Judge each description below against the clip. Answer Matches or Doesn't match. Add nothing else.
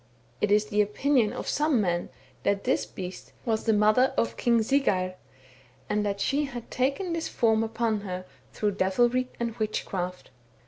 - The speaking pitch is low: Doesn't match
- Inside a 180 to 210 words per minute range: Doesn't match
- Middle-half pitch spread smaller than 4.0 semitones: Matches